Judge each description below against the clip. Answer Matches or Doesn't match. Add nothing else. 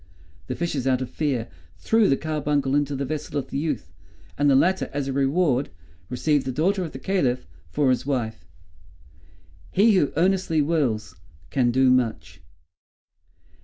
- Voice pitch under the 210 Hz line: Matches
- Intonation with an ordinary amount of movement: Matches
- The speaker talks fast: Doesn't match